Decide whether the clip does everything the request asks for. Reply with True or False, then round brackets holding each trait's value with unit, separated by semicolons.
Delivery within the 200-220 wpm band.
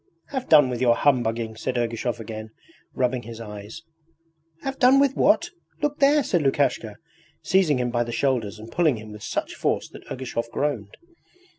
False (170 wpm)